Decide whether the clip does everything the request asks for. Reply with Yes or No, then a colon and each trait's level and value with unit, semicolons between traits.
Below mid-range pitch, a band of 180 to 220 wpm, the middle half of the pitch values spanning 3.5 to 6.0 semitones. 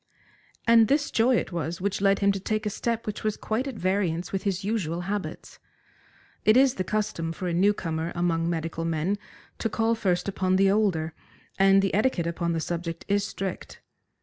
No: high, 195 Hz; average, 195 wpm; average, 3.8 semitones